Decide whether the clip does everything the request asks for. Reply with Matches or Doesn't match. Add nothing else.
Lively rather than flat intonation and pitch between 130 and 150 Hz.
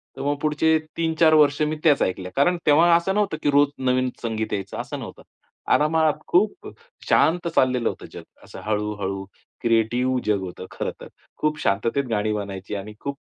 Matches